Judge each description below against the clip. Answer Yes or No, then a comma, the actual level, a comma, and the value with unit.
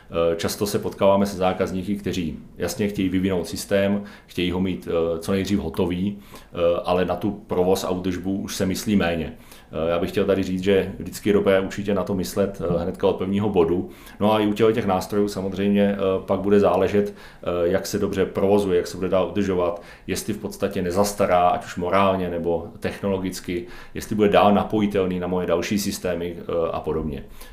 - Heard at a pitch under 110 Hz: Yes, very low, 95 Hz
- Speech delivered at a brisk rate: Yes, fast, 175 wpm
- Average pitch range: No, narrow, 2.2 semitones